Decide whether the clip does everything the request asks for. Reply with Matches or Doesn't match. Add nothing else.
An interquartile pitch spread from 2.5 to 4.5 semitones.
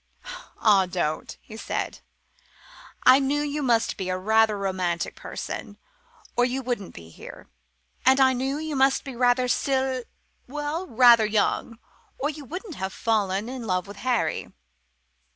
Doesn't match